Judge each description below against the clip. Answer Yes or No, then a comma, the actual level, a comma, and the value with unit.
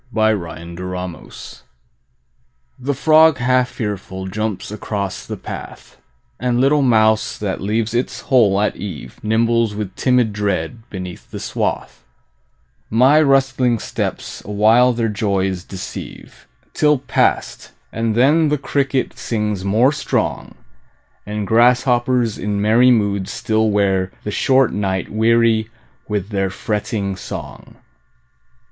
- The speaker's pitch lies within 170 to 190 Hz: No, low, 110 Hz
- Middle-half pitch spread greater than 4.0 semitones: No, average, 3.7 semitones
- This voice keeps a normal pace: No, slow, 120 wpm